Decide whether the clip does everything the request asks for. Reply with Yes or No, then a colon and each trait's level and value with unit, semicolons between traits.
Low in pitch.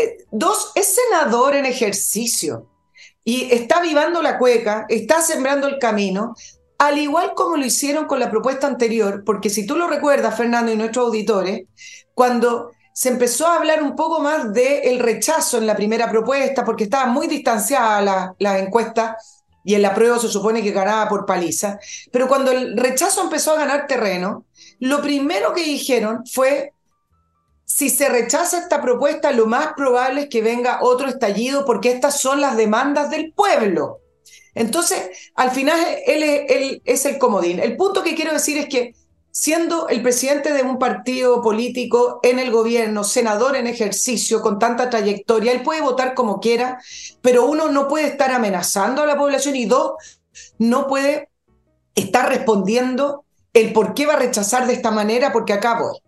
No: very high, 250 Hz